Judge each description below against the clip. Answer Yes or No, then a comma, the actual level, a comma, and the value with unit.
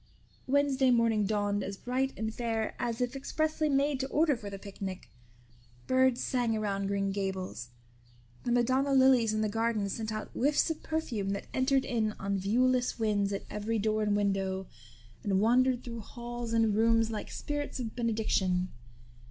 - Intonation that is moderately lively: Yes, average, 4.0 semitones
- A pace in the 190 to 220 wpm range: No, average, 165 wpm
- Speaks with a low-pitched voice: No, high, 225 Hz